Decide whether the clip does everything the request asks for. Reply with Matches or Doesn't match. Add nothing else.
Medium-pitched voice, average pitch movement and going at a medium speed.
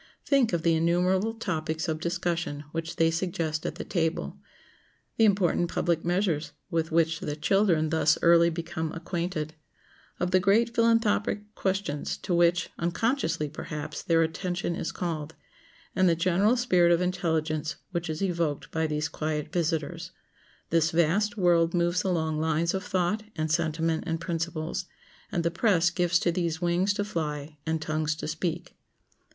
Doesn't match